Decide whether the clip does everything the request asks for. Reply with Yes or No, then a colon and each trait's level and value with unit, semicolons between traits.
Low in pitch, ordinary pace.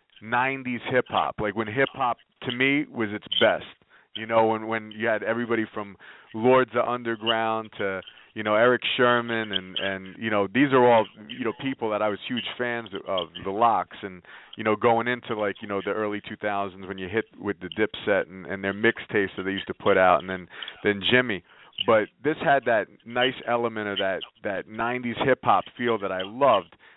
No: low, 110 Hz; fast, 210 wpm